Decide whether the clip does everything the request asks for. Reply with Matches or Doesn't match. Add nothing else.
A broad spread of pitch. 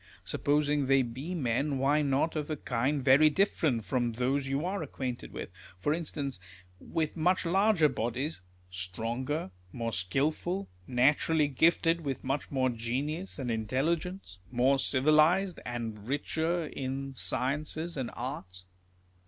Doesn't match